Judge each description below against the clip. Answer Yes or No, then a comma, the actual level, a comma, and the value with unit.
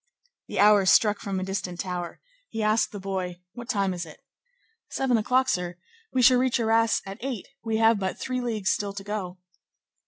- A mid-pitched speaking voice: No, high, 210 Hz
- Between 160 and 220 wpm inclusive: Yes, average, 190 wpm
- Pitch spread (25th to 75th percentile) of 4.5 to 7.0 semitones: No, average, 3.3 semitones